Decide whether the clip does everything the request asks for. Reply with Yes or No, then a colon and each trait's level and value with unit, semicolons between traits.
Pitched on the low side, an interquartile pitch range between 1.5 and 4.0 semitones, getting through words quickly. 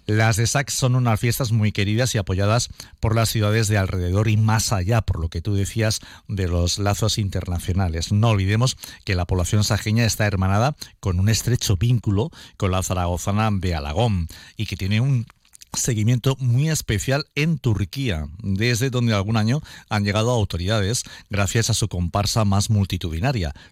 No: low, 110 Hz; average, 3.2 semitones; average, 170 wpm